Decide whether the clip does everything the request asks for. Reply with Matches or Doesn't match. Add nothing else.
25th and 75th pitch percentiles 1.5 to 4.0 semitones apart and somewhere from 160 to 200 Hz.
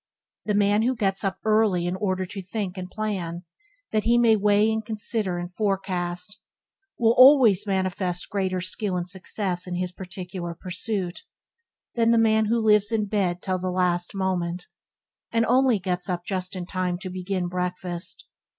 Matches